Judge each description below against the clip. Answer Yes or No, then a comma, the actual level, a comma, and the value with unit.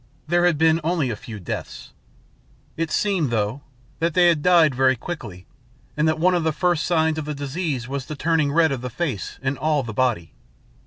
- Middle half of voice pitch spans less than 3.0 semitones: No, average, 4.4 semitones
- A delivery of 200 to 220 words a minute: Yes, fast, 205 wpm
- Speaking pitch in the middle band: Yes, medium, 150 Hz